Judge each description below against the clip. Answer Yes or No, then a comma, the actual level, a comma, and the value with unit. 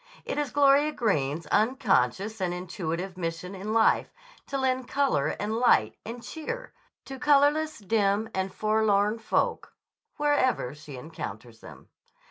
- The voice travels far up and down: Yes, wide, 7.0 semitones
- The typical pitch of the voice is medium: No, high, 215 Hz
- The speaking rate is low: Yes, slow, 130 wpm